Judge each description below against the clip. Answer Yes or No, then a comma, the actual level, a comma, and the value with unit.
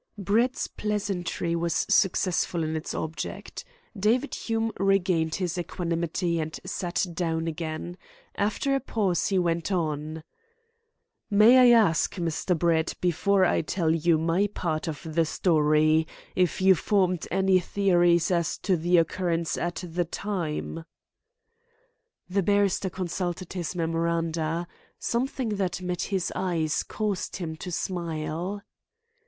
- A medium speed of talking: No, slow, 125 wpm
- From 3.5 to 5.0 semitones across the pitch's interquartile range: No, average, 3.0 semitones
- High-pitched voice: No, medium, 175 Hz